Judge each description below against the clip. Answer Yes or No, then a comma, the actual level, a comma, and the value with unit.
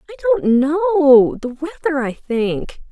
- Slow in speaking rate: Yes, slow, 125 wpm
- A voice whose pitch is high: Yes, very high, 275 Hz